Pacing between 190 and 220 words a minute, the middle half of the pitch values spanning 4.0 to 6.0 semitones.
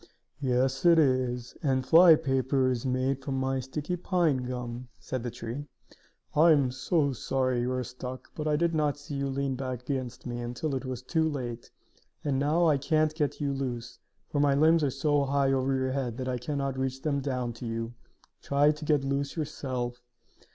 No: average, 195 wpm; narrow, 2.5 semitones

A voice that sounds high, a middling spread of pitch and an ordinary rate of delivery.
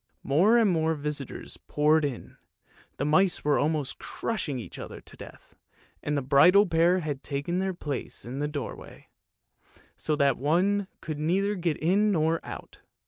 No: medium, 155 Hz; average, 4.1 semitones; average, 160 wpm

